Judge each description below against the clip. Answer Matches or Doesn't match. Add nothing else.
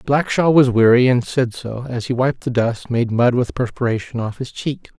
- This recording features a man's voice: Matches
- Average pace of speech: Doesn't match